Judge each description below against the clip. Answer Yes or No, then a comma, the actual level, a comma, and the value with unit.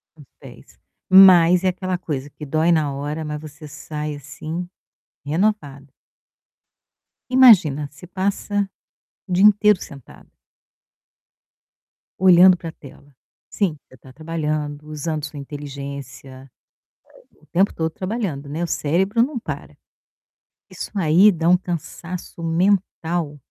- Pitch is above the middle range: No, medium, 160 Hz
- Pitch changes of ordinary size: Yes, average, 4.0 semitones